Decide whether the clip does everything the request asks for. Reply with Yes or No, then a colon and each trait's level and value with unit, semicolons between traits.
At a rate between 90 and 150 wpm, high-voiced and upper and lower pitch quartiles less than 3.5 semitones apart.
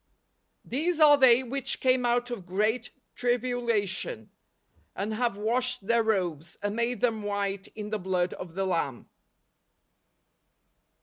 No: average, 140 wpm; high, 220 Hz; average, 4.1 semitones